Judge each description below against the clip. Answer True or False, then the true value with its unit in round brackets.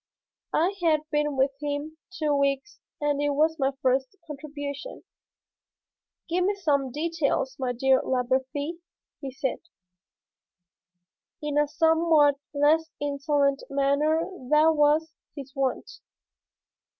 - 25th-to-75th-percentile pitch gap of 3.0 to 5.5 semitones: False (2.4 semitones)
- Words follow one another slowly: True (115 wpm)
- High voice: True (290 Hz)